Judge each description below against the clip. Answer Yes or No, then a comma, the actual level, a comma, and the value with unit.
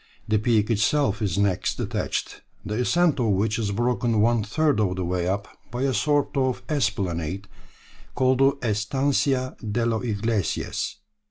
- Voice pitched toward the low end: Yes, low, 110 Hz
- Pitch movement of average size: Yes, average, 4.2 semitones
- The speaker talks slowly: No, average, 155 wpm